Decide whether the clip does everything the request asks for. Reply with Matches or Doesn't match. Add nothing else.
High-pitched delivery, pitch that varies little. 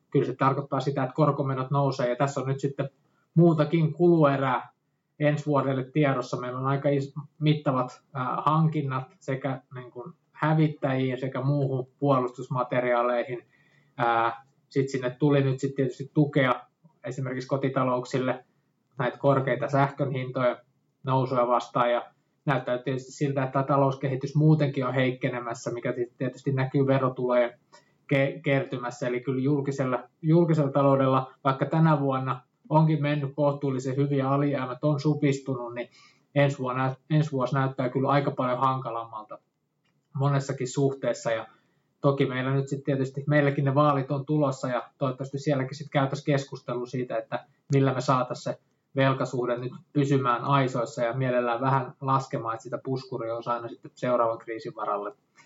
Doesn't match